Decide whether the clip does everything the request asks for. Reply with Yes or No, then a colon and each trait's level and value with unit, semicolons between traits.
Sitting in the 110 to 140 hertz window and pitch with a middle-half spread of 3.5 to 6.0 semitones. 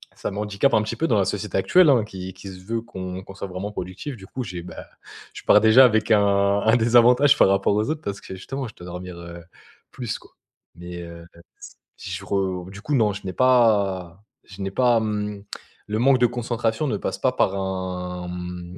No: low, 100 Hz; average, 3.9 semitones